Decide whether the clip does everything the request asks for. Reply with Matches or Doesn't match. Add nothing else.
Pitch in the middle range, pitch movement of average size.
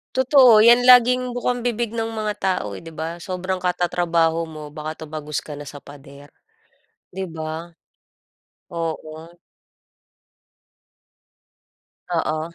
Doesn't match